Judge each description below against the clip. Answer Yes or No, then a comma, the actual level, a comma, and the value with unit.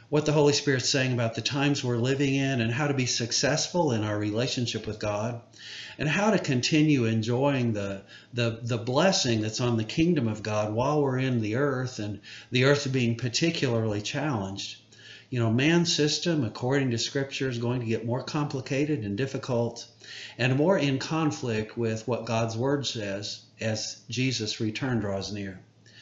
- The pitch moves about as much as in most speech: Yes, average, 4.0 semitones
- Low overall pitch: Yes, low, 125 Hz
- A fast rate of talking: No, average, 175 wpm